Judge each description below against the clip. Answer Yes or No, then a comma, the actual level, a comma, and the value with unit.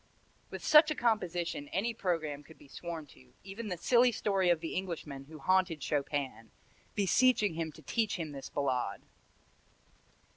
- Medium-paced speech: Yes, average, 155 wpm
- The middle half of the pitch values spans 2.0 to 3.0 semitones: No, wide, 5.5 semitones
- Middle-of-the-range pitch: Yes, medium, 170 Hz